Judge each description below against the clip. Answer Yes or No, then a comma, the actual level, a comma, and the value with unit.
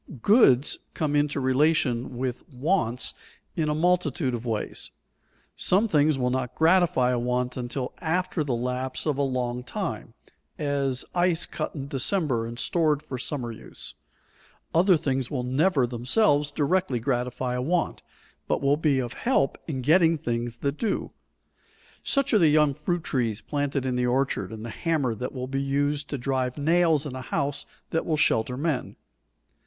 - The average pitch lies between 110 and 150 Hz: Yes, medium, 140 Hz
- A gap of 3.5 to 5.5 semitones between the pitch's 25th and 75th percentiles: Yes, average, 3.9 semitones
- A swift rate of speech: No, average, 170 wpm